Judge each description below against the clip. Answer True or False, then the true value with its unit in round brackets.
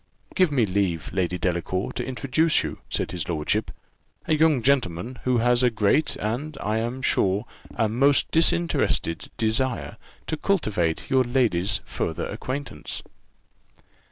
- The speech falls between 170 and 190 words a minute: False (140 wpm)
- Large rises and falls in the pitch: True (6.4 semitones)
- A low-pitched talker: True (120 Hz)